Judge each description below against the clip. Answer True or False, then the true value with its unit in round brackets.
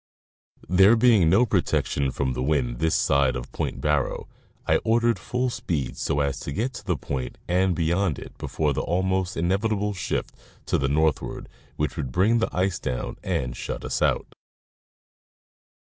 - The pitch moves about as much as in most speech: False (6.3 semitones)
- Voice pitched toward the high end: False (85 Hz)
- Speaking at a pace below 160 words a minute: False (165 wpm)